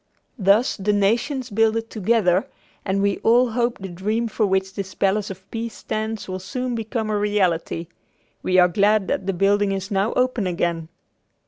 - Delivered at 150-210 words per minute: Yes, average, 175 wpm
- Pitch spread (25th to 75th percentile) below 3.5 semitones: Yes, average, 2.8 semitones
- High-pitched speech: Yes, high, 205 Hz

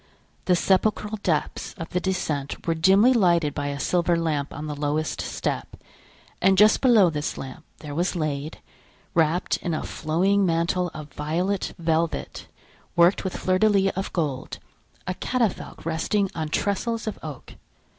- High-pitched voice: No, medium, 170 Hz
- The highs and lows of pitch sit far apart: No, average, 3.8 semitones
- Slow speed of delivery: No, average, 155 wpm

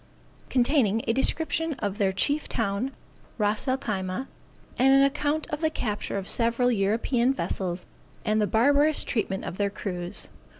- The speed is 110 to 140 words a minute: No, average, 155 wpm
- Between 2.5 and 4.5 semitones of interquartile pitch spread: No, average, 5.3 semitones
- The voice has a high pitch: Yes, high, 230 Hz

